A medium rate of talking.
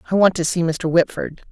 No: fast, 235 wpm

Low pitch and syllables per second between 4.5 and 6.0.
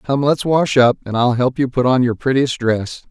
Yes: low, 130 Hz; 4.9 syllables/s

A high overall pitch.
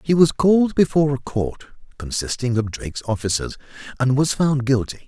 No: low, 135 Hz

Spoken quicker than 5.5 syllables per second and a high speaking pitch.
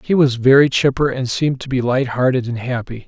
No: 5.7 syllables/s; low, 130 Hz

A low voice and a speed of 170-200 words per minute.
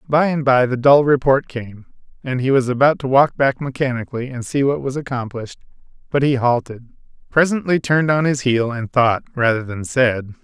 Yes: low, 130 Hz; average, 190 wpm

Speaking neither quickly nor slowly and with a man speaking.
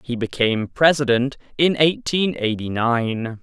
No: slow, 125 wpm; male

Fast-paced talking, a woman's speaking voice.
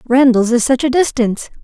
No: average, 185 wpm; female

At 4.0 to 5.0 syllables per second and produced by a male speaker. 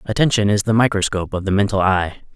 No: 6.5 syllables/s; male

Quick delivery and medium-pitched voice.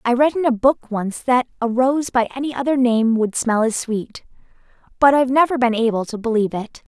No: fast, 215 wpm; high, 245 Hz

